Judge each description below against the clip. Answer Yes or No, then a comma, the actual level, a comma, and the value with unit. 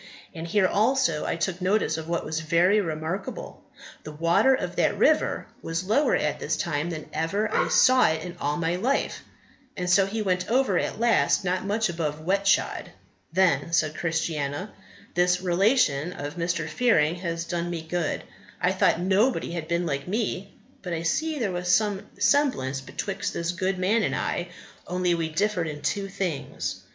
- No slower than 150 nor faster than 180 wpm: Yes, average, 175 wpm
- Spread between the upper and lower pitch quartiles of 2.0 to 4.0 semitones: Yes, average, 3.5 semitones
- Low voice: No, medium, 180 Hz